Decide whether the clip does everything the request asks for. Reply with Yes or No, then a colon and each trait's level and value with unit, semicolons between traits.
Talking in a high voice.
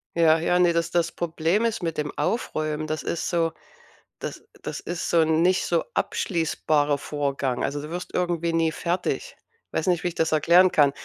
No: medium, 165 Hz